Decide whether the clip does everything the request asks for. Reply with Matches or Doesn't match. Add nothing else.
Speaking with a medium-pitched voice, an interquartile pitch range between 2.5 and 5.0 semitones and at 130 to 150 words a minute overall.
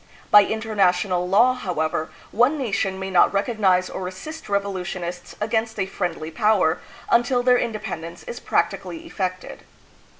Doesn't match